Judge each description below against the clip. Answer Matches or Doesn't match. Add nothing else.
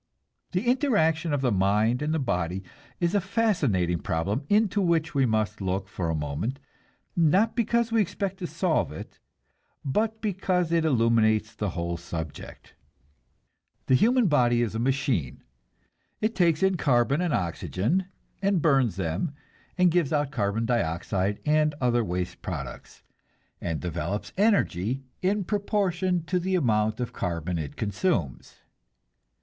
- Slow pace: Doesn't match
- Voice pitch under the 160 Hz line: Matches